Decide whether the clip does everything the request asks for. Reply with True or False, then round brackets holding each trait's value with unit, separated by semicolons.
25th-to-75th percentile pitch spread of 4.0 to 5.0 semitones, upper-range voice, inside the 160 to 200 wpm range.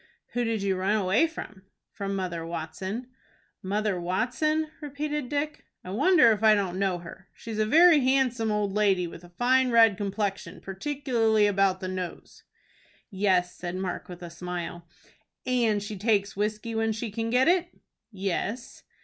True (4.5 semitones; 210 Hz; 165 wpm)